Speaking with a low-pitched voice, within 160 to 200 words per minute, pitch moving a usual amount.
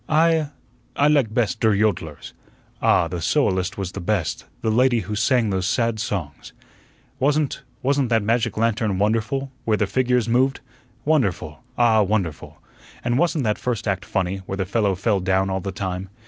Yes: low, 110 Hz; average, 170 wpm; average, 4.5 semitones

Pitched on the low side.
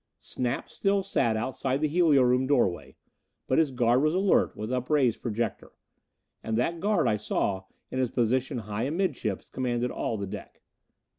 Yes: low, 125 Hz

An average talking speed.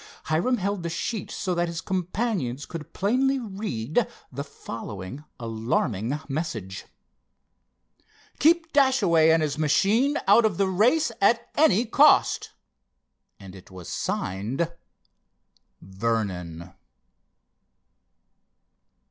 No: slow, 100 wpm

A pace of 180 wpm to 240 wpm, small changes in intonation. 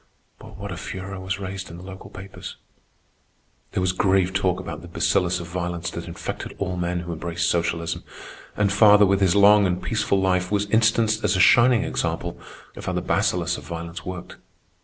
Yes: average, 190 wpm; narrow, 2.3 semitones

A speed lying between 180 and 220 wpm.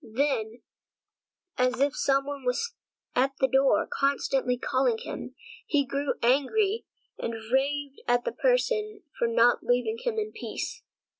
No: average, 145 wpm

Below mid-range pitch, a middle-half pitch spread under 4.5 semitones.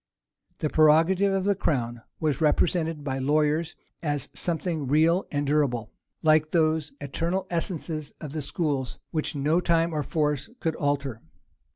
No: medium, 155 Hz; narrow, 2.5 semitones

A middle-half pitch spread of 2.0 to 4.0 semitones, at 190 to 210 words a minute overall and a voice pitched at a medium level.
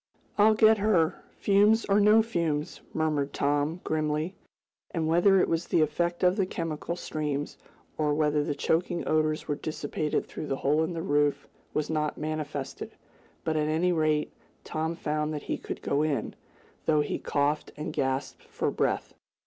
No: narrow, 2.5 semitones; average, 165 wpm; medium, 155 Hz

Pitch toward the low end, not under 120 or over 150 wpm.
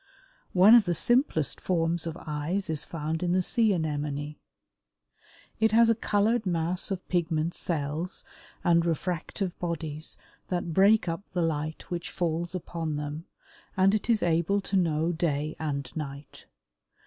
No: medium, 170 Hz; average, 145 wpm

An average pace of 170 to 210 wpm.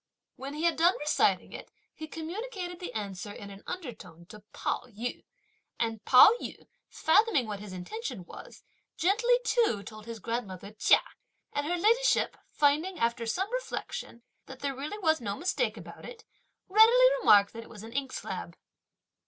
No: average, 160 wpm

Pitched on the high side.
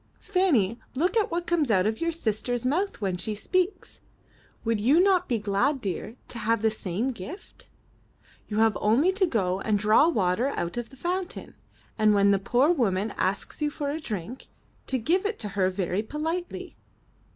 Yes: high, 230 Hz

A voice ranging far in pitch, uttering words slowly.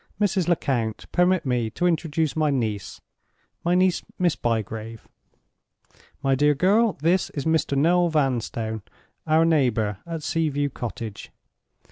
Yes: wide, 6.5 semitones; slow, 125 wpm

